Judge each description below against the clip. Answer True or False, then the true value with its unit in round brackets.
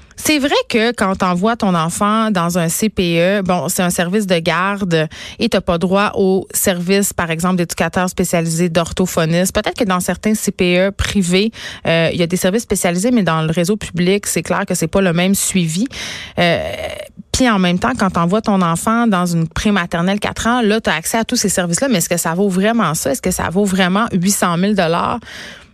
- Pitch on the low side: False (190 Hz)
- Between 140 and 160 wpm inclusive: False (210 wpm)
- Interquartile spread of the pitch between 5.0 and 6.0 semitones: False (3.2 semitones)